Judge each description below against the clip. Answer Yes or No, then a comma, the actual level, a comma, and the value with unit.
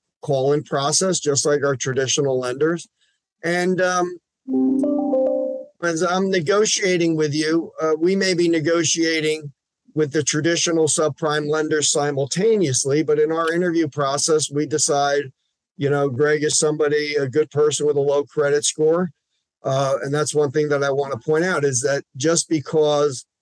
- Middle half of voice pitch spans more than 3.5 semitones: No, average, 2.8 semitones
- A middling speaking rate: Yes, average, 155 wpm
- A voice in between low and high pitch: Yes, medium, 155 Hz